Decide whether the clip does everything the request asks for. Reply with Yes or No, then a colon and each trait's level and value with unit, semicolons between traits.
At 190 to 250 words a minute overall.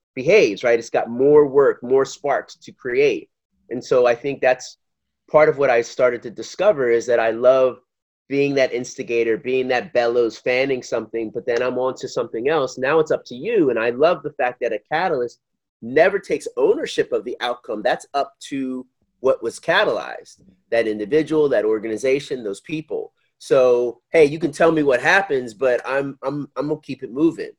Yes: average, 195 wpm